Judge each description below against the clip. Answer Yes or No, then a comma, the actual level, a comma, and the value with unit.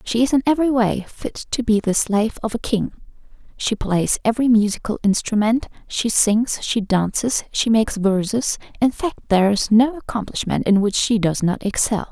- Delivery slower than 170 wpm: No, average, 185 wpm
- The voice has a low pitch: No, high, 220 Hz